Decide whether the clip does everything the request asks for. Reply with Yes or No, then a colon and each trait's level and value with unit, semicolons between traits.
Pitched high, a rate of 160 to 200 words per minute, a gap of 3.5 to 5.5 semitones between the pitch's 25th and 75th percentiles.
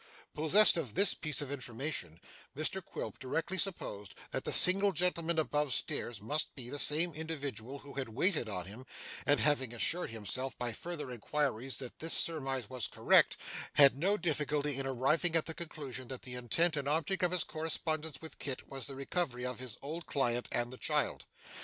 No: medium, 145 Hz; average, 185 wpm; average, 4.2 semitones